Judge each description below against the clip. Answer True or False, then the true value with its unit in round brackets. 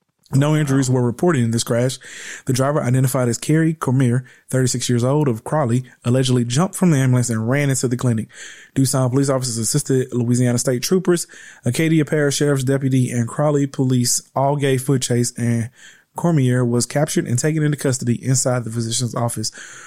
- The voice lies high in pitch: False (130 Hz)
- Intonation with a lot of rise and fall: False (3.1 semitones)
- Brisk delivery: False (175 wpm)